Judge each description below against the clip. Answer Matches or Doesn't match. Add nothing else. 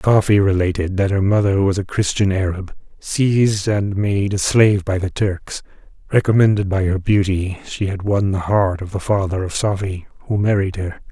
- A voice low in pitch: Matches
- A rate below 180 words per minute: Doesn't match